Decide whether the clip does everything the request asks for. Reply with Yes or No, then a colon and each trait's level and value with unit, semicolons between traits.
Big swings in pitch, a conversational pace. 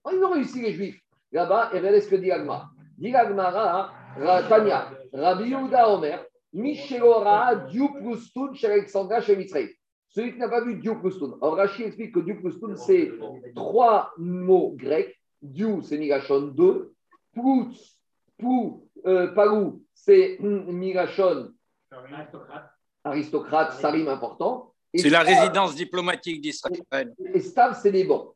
No: wide, 7.5 semitones; slow, 135 wpm